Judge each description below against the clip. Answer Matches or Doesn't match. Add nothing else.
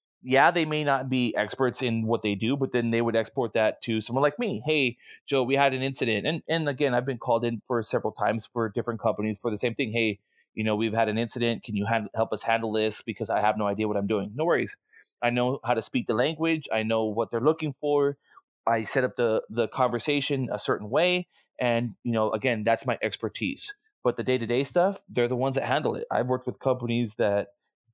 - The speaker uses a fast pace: Matches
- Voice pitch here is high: Doesn't match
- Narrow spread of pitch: Doesn't match